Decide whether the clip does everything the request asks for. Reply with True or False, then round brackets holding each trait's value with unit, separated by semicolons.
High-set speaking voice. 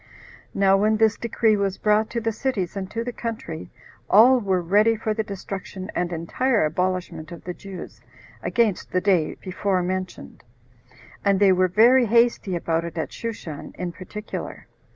True (195 Hz)